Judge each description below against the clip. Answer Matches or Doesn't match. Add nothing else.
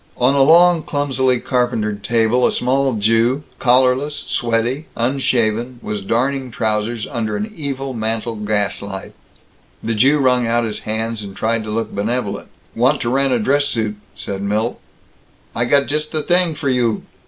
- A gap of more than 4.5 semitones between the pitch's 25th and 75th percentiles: Doesn't match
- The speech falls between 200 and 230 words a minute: Doesn't match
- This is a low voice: Matches